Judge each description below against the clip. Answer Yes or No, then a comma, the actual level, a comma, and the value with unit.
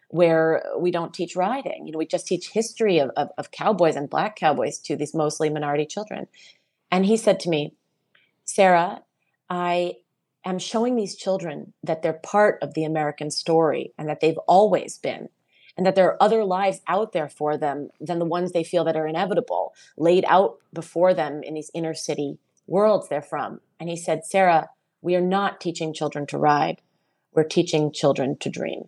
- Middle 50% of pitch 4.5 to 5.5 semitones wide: No, average, 3.2 semitones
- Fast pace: No, average, 190 wpm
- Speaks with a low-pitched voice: No, medium, 170 Hz